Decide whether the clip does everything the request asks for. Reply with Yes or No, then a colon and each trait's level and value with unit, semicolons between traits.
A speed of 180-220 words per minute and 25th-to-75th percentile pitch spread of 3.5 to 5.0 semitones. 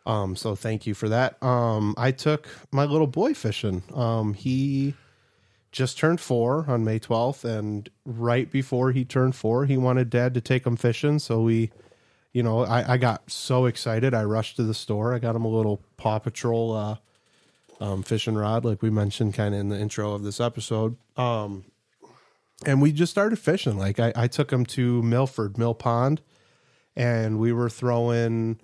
No: average, 185 wpm; narrow, 2.5 semitones